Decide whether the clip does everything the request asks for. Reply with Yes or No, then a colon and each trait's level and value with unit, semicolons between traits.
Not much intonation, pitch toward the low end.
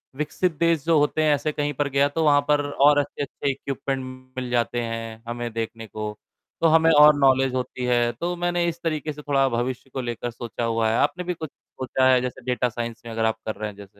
No: average, 3.9 semitones; low, 130 Hz